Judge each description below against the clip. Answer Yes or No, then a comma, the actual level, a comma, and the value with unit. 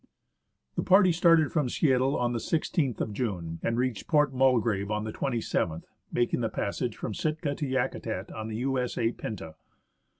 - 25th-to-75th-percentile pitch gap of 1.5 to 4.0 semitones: No, average, 4.6 semitones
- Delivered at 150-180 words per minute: Yes, average, 165 wpm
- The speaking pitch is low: Yes, low, 125 Hz